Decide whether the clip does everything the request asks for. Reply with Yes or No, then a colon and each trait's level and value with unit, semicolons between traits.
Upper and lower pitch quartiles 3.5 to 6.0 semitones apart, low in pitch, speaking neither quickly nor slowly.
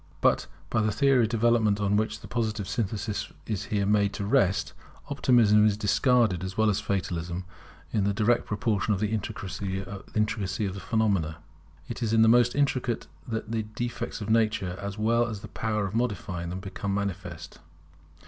No: narrow, 2.5 semitones; low, 105 Hz; average, 180 wpm